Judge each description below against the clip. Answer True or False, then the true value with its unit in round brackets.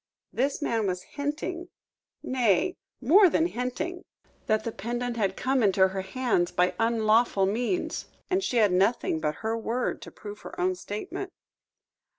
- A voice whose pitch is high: True (230 Hz)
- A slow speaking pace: False (155 wpm)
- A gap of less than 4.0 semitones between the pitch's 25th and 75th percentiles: False (5.3 semitones)